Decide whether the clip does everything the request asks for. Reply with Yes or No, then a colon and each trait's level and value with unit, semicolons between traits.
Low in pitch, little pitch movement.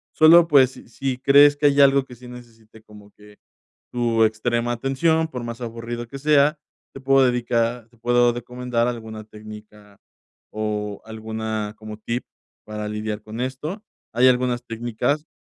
No: low, 120 Hz; average, 3.2 semitones